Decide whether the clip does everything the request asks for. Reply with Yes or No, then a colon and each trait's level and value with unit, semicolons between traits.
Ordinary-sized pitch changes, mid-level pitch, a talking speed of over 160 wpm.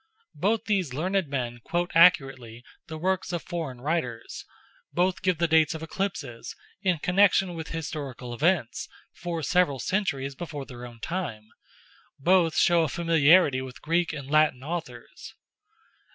No: average, 4.8 semitones; medium, 160 Hz; average, 140 wpm